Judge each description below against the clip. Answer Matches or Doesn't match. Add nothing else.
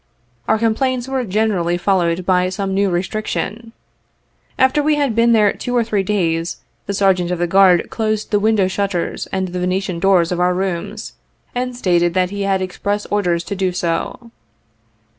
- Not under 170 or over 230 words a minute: Matches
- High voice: Matches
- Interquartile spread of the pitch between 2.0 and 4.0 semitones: Matches